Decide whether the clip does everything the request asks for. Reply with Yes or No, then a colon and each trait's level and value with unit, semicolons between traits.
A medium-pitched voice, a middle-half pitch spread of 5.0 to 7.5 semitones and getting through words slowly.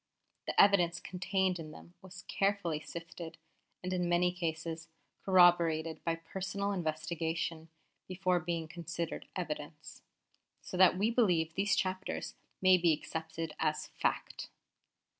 No: medium, 175 Hz; narrow, 2.4 semitones; slow, 120 wpm